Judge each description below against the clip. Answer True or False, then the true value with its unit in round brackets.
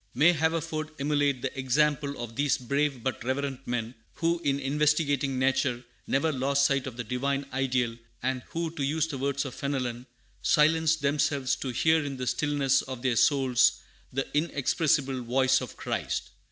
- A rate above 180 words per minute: False (165 wpm)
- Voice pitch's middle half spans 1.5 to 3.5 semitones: True (2.4 semitones)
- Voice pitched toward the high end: False (140 Hz)